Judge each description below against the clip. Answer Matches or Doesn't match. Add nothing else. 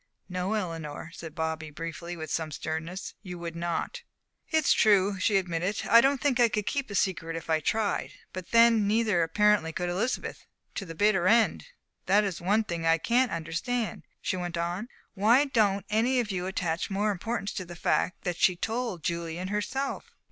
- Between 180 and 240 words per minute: Matches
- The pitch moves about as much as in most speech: Matches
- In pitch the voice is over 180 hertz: Matches